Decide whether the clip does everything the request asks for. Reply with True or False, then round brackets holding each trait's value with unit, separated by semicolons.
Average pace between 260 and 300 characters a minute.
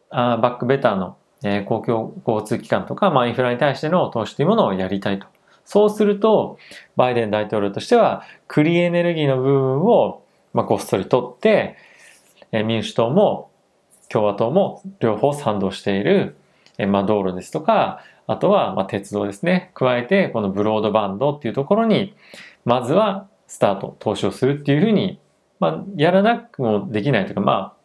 False (350 characters per minute)